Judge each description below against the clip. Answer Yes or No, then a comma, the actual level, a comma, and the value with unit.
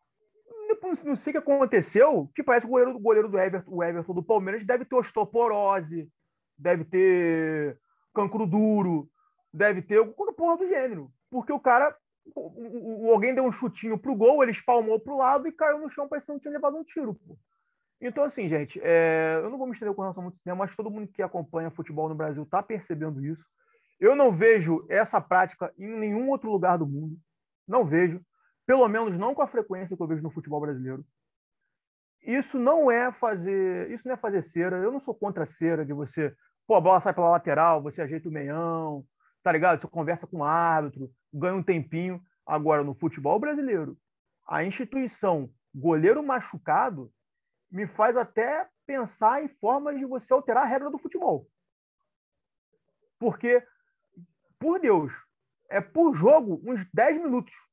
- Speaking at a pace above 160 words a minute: Yes, average, 180 wpm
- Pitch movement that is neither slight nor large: No, wide, 7.7 semitones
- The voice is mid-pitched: No, high, 215 Hz